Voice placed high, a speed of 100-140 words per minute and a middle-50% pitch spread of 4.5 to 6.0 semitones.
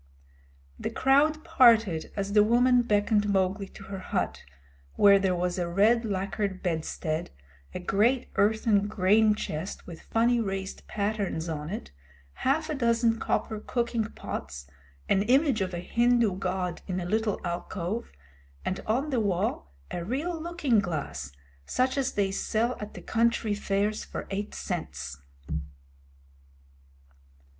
No: high, 210 Hz; slow, 135 wpm; average, 3.9 semitones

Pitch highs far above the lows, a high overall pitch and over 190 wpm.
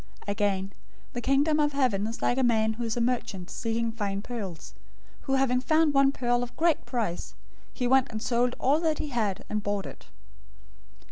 No: average, 4.1 semitones; high, 240 Hz; average, 200 wpm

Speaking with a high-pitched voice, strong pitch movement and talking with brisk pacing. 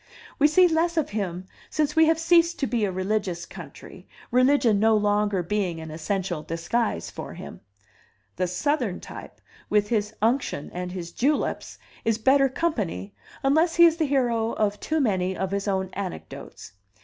No: high, 215 Hz; wide, 7.2 semitones; average, 165 wpm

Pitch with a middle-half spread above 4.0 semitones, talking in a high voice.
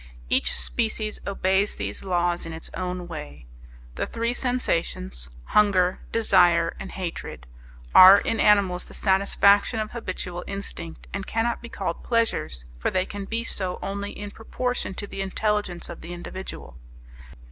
No: average, 3.2 semitones; high, 195 Hz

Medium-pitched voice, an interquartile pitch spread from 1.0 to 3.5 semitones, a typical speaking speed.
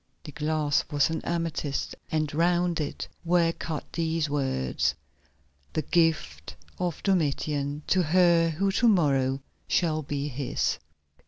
No: medium, 155 Hz; average, 2.9 semitones; slow, 130 wpm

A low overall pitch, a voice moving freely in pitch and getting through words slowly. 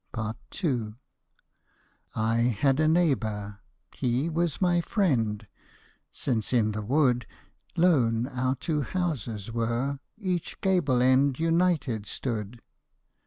Yes: low, 130 Hz; wide, 6.0 semitones; slow, 110 wpm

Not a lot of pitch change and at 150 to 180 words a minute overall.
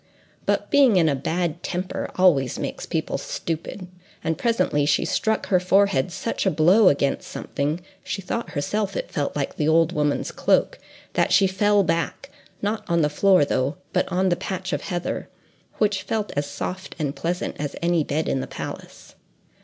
No: average, 4.6 semitones; average, 170 wpm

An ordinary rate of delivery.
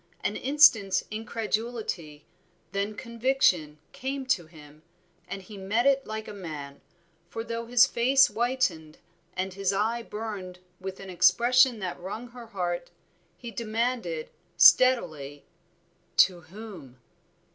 No: slow, 125 wpm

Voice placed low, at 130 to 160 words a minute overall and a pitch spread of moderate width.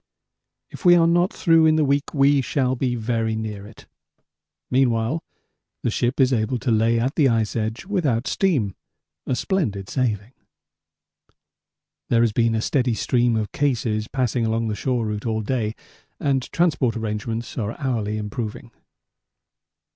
Yes: low, 120 Hz; average, 155 wpm; average, 3.6 semitones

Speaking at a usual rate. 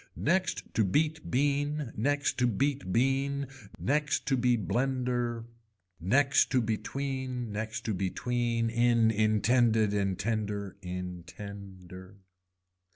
No: slow, 105 wpm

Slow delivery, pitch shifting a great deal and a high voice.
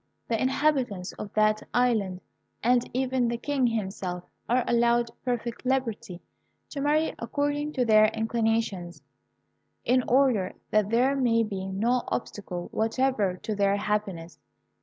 No: slow, 130 wpm; average, 3.7 semitones; high, 230 Hz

